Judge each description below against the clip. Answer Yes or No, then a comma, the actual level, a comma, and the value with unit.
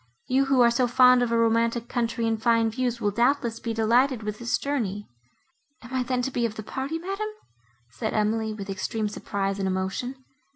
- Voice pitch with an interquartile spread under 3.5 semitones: Yes, narrow, 2.6 semitones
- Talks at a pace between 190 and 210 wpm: Yes, average, 200 wpm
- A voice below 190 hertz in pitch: No, high, 230 Hz